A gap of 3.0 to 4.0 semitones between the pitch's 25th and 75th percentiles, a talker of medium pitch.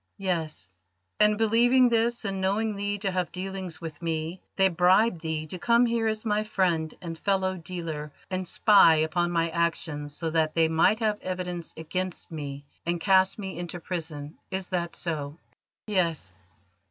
Yes: average, 3.6 semitones; medium, 180 Hz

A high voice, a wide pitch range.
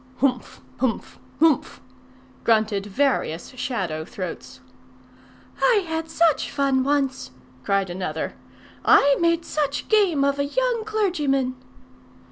Yes: very high, 275 Hz; wide, 6.6 semitones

